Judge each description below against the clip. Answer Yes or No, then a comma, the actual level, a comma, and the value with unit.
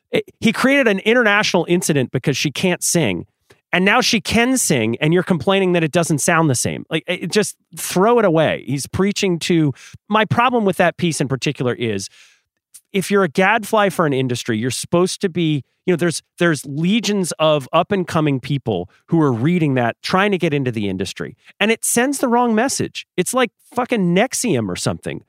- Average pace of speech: Yes, average, 195 wpm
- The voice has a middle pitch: Yes, medium, 175 Hz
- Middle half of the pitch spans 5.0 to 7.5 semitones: Yes, wide, 5.5 semitones